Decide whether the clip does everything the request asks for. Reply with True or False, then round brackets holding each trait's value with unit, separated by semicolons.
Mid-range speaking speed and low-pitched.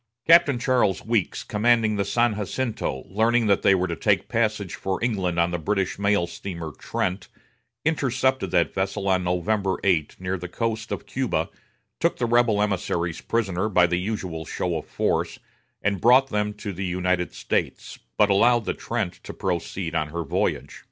True (170 wpm; 100 Hz)